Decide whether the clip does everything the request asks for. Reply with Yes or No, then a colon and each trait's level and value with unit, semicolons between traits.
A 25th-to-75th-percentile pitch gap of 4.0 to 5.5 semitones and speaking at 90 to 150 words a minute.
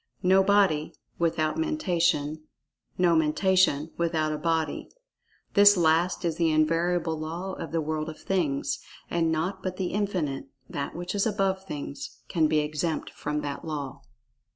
No: average, 3.1 semitones; average, 140 wpm